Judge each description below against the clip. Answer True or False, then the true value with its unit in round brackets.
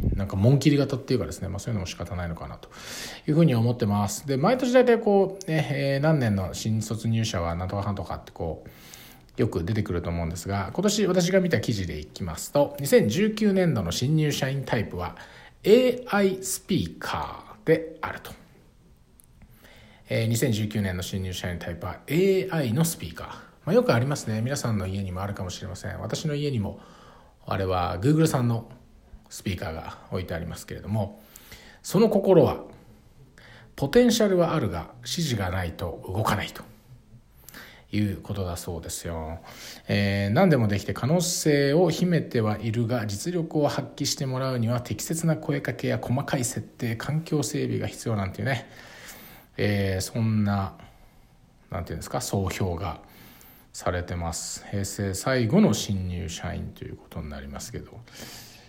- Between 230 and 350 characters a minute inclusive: True (330 characters per minute)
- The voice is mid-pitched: False (115 Hz)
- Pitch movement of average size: False (7.1 semitones)